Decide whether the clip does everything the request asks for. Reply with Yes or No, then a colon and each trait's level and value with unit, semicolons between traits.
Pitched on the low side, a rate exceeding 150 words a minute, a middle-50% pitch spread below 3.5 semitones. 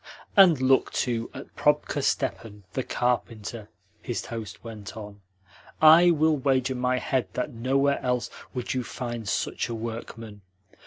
No: low, 125 Hz; average, 145 wpm; average, 2.8 semitones